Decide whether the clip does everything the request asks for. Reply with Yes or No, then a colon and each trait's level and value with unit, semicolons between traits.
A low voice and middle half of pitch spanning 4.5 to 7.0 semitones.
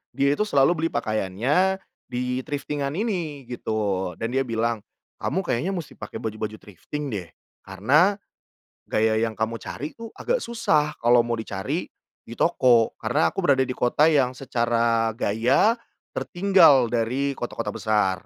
Yes: low, 125 Hz; average, 5.3 semitones